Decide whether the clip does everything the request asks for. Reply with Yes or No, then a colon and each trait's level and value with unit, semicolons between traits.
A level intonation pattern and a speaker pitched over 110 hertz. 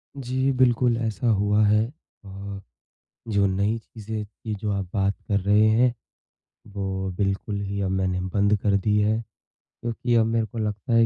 No: narrow, 2.3 semitones; low, 105 Hz